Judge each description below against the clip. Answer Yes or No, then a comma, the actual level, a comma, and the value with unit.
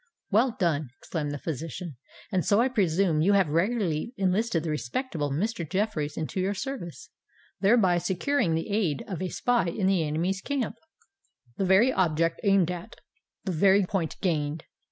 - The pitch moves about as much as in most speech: Yes, average, 4.2 semitones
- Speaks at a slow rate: No, average, 155 wpm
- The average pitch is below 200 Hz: Yes, medium, 185 Hz